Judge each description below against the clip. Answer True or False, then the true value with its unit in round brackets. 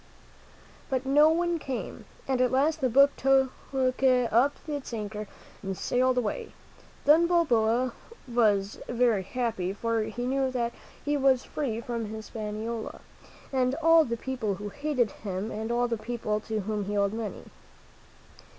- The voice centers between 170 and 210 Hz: False (240 Hz)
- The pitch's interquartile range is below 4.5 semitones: True (3.6 semitones)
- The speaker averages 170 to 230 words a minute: False (150 wpm)